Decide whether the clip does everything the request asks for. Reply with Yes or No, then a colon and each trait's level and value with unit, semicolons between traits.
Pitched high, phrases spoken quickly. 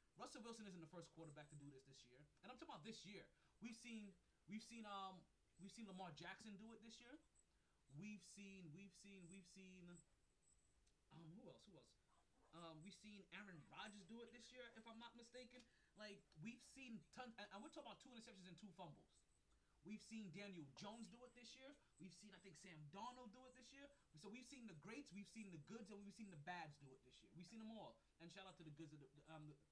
Yes: high, 200 Hz; fast, 240 wpm